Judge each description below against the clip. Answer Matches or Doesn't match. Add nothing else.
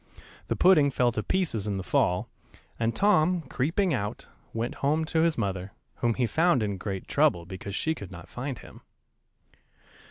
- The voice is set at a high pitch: Doesn't match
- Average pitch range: Doesn't match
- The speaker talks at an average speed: Matches